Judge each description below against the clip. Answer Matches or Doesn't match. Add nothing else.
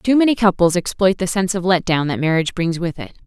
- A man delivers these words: Doesn't match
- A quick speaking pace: Matches